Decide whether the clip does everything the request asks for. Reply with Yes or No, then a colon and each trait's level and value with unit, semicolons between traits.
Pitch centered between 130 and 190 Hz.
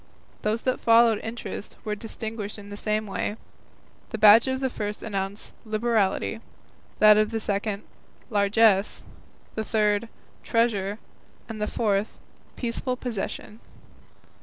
No: high, 215 Hz